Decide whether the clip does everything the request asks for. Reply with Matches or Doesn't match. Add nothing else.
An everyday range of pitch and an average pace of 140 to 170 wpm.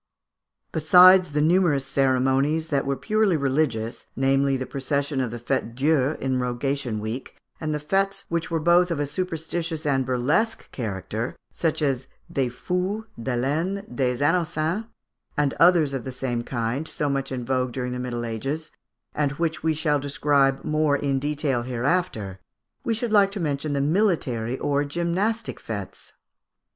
Matches